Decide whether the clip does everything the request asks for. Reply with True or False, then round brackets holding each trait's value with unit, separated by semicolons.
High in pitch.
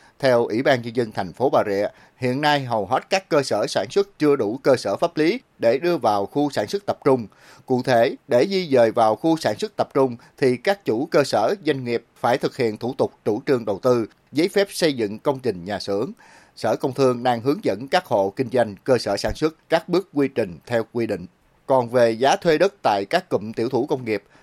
False (130 Hz)